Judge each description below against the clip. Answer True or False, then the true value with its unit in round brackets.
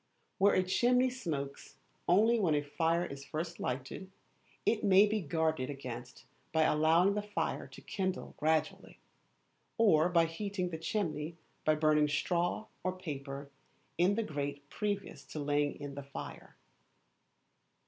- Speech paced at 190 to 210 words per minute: False (140 wpm)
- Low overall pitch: False (165 Hz)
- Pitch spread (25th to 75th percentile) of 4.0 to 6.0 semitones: True (4.8 semitones)